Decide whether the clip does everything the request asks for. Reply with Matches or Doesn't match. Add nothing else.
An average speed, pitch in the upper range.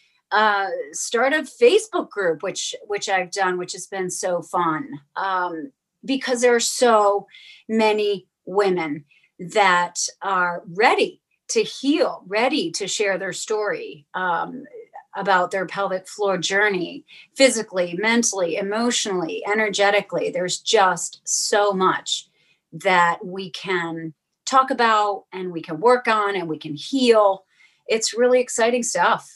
Doesn't match